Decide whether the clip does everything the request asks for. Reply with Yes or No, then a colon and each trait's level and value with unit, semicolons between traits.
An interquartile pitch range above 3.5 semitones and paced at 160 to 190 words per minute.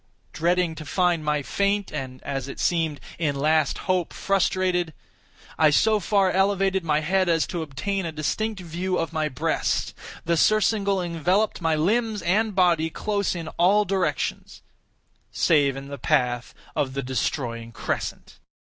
No: average, 4.2 semitones; average, 150 wpm